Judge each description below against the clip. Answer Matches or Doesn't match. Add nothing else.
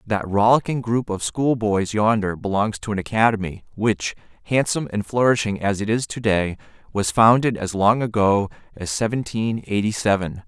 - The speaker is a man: Matches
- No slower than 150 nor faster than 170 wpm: Matches